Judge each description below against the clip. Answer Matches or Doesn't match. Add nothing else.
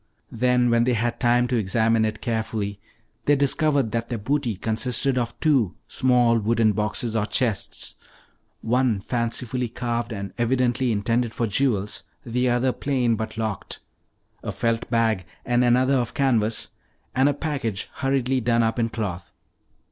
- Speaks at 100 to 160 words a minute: Matches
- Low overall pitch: Matches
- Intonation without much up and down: Matches